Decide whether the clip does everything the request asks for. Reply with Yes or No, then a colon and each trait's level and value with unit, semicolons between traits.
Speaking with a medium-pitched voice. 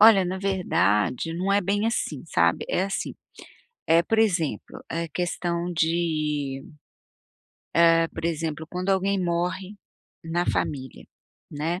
Yes: medium, 170 Hz